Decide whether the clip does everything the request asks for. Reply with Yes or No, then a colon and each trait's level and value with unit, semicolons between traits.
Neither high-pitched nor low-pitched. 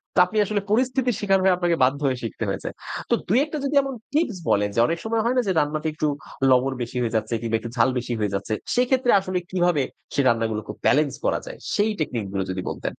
Yes: medium, 165 Hz